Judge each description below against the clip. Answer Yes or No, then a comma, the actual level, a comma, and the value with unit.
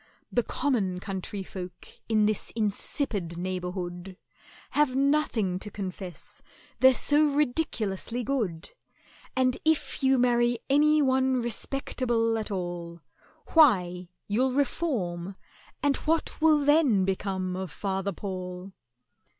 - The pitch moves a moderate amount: No, wide, 6.3 semitones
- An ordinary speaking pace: No, slow, 110 wpm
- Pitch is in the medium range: No, high, 215 Hz